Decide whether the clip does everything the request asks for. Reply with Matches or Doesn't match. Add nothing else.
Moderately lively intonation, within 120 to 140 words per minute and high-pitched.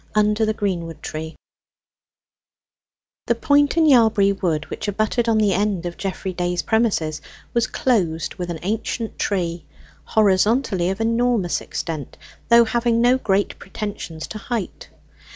Matches